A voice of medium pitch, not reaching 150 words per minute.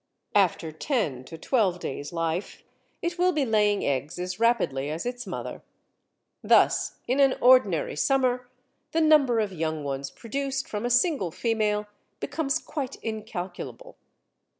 No: high, 220 Hz; average, 140 wpm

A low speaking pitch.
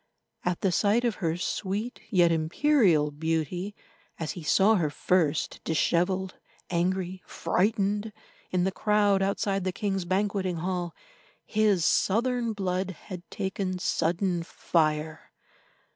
No: medium, 185 Hz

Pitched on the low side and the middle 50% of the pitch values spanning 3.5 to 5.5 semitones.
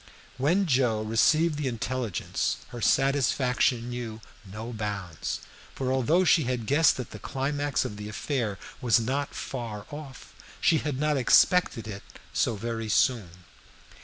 Yes: low, 125 Hz; average, 4.6 semitones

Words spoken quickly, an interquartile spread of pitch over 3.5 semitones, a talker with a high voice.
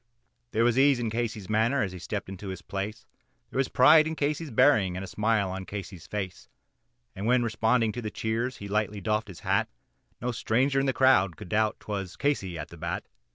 No: fast, 210 wpm; average, 4.2 semitones; low, 110 Hz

